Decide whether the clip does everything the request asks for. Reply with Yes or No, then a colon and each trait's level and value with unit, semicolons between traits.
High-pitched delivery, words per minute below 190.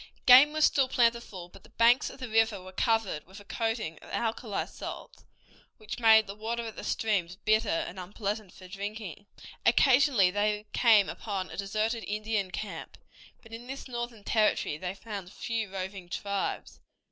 Yes: high, 215 Hz; average, 170 wpm